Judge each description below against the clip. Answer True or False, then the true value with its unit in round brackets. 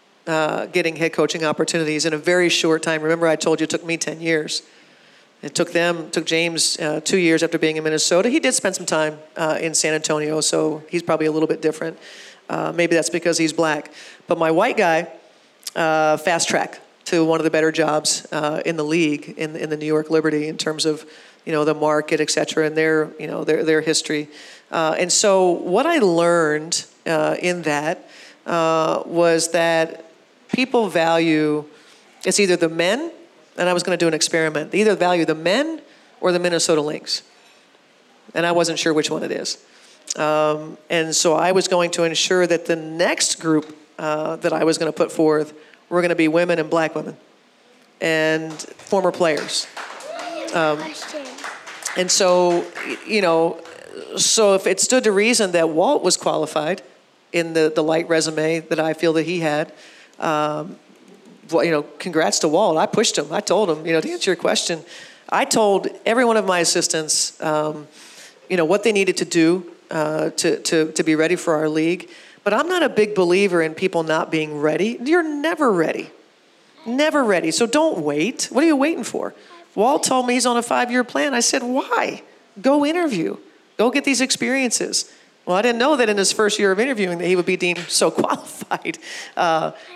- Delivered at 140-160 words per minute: False (200 wpm)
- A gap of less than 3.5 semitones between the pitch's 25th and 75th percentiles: True (3.1 semitones)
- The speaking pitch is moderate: True (165 Hz)